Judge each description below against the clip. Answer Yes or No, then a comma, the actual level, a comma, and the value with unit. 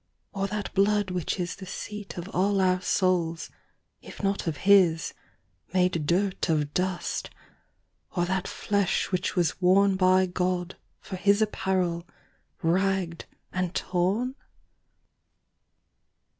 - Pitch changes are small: Yes, narrow, 2.0 semitones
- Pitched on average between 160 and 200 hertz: Yes, medium, 185 Hz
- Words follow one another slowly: Yes, slow, 110 wpm